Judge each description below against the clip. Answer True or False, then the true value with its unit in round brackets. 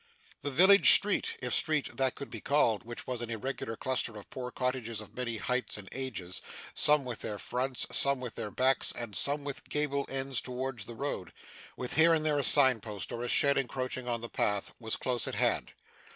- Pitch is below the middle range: True (130 Hz)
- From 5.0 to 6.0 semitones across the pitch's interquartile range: False (3.2 semitones)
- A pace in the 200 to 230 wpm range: True (205 wpm)